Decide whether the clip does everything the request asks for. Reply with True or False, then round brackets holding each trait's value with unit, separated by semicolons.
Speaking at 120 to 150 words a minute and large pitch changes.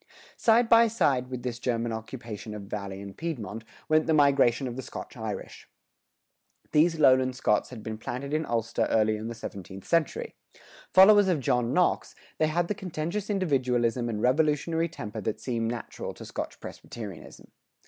False (165 wpm; 6.0 semitones)